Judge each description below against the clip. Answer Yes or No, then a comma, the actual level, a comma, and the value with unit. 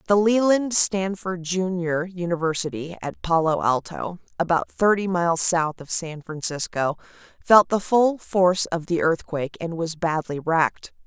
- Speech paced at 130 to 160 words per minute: Yes, average, 140 wpm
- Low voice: No, medium, 175 Hz